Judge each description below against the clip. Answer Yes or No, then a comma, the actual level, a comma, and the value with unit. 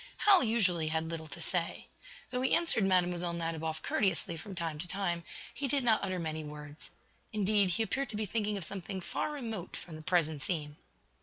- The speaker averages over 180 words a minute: Yes, average, 190 wpm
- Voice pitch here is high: No, medium, 180 Hz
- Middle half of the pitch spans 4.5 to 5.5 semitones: Yes, average, 4.9 semitones